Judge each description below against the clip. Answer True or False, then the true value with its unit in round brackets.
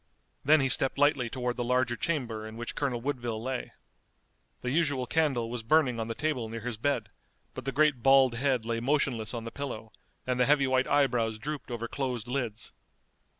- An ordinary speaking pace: True (195 wpm)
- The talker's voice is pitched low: True (125 Hz)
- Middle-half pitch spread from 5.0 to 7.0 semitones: False (3.1 semitones)